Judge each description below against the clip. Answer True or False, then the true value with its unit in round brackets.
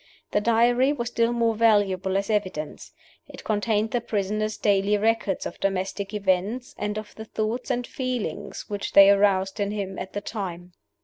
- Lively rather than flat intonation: False (2.5 semitones)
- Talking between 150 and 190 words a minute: True (170 wpm)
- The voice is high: True (210 Hz)